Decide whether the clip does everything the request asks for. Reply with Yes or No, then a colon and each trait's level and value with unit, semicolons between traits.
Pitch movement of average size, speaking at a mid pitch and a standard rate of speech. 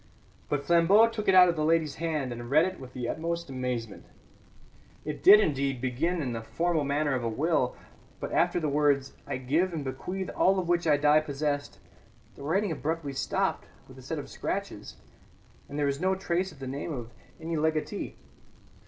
Yes: average, 3.9 semitones; medium, 150 Hz; average, 195 wpm